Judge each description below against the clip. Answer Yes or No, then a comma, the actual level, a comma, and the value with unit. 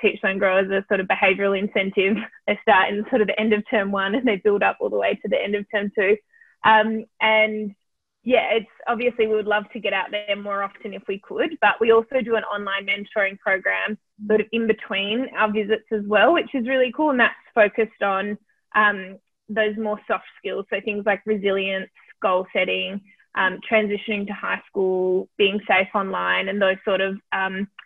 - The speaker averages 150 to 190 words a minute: No, fast, 205 wpm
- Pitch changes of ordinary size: No, narrow, 1.9 semitones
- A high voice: Yes, high, 210 Hz